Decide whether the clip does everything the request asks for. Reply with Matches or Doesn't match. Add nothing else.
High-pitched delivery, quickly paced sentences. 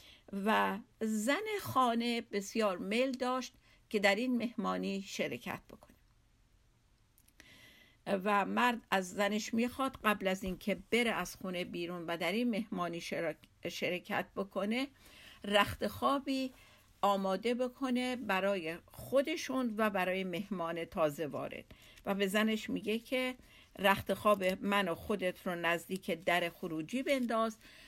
Doesn't match